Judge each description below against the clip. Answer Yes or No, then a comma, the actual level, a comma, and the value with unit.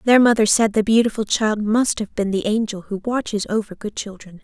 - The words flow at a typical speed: No, fast, 215 wpm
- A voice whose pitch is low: No, high, 215 Hz